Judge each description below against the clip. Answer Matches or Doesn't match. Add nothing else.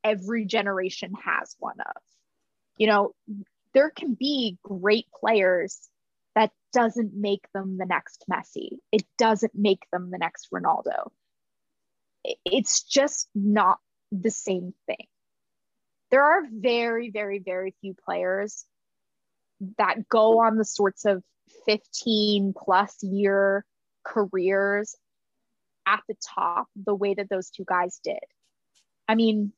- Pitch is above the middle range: Matches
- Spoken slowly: Matches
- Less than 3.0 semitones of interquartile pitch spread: Matches